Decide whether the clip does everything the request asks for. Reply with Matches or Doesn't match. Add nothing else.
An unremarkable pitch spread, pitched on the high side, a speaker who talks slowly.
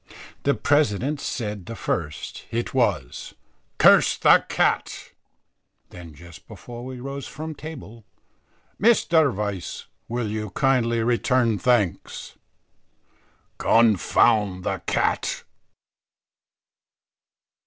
Doesn't match